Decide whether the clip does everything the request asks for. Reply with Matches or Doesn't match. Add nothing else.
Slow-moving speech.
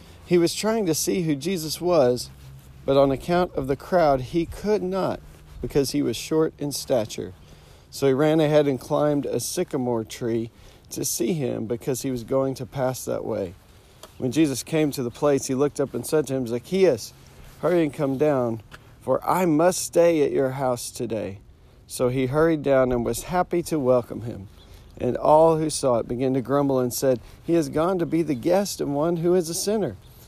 Doesn't match